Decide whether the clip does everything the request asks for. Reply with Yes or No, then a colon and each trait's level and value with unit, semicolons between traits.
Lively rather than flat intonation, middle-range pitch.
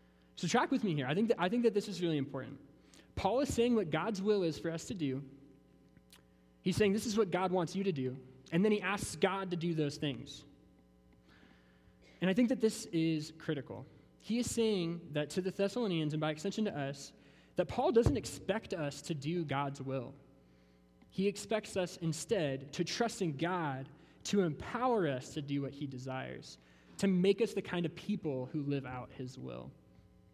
Yes: wide, 6.6 semitones; medium, 160 Hz